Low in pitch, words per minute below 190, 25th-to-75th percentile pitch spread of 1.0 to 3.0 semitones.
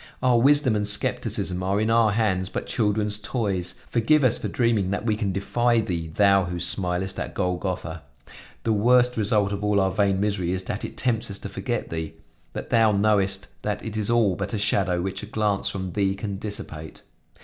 No: low, 100 Hz; average, 200 wpm; average, 2.7 semitones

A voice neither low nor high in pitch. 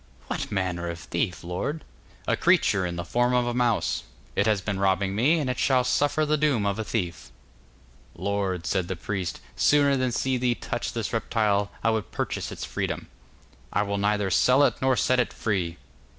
No: low, 105 Hz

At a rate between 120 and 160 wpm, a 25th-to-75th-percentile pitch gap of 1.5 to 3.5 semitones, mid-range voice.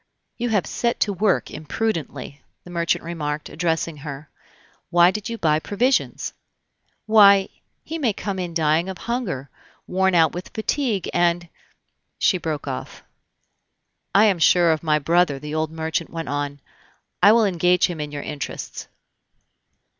No: average, 155 wpm; average, 4.5 semitones; medium, 170 Hz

